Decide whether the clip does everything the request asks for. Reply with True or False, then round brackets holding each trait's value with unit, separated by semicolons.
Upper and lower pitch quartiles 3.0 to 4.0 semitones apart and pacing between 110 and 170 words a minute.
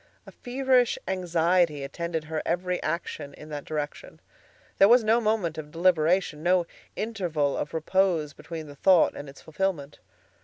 True (3.7 semitones; 150 wpm)